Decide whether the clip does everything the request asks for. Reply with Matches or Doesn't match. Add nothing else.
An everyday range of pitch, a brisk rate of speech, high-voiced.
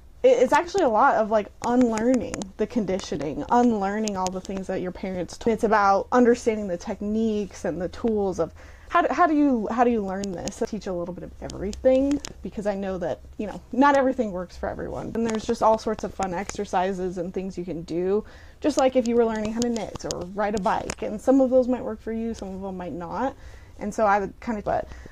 Matches